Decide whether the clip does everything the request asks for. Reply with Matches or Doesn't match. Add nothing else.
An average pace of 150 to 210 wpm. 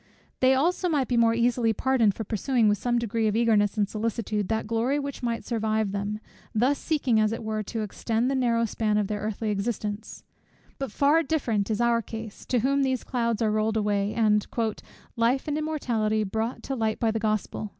Matches